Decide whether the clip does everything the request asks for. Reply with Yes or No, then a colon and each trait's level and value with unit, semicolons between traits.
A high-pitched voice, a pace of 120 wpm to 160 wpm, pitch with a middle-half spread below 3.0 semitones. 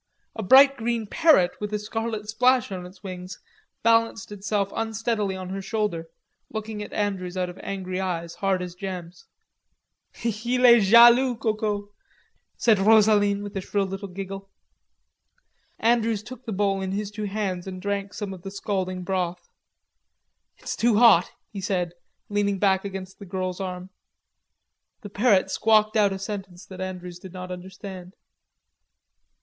Yes: high, 200 Hz; average, 155 wpm; narrow, 2.6 semitones